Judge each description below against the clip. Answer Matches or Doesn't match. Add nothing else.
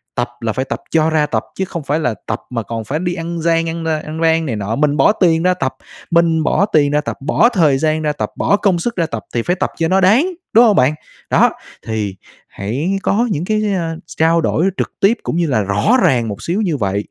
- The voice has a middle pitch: Matches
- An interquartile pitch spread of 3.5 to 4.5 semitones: Doesn't match